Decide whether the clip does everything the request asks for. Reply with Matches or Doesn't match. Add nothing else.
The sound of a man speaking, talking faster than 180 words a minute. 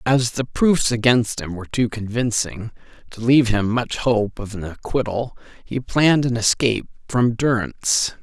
Doesn't match